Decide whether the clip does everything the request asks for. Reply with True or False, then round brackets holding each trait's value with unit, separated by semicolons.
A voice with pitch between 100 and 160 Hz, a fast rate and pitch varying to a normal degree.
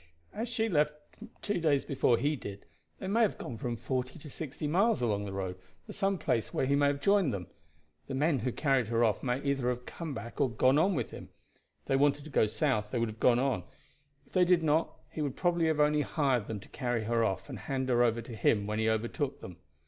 True (135 Hz; 240 wpm; 4.7 semitones)